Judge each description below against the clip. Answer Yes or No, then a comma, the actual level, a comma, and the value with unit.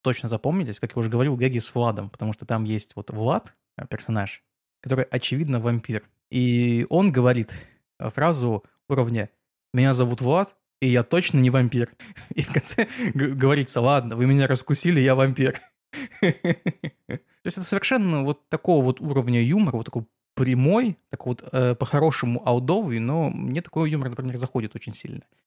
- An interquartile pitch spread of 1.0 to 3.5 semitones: No, average, 4.6 semitones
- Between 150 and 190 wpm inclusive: Yes, average, 155 wpm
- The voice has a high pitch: No, low, 130 Hz